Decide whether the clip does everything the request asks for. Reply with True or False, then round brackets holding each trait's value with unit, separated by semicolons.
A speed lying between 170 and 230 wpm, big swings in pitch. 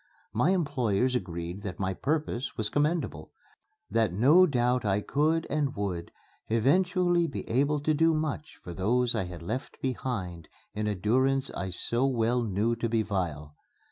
False (160 wpm; 6.5 semitones)